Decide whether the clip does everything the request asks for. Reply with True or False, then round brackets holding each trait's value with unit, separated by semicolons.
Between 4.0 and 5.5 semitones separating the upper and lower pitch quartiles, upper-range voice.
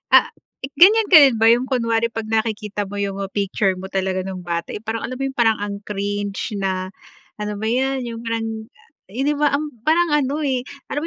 True (4.8 semitones; 225 Hz)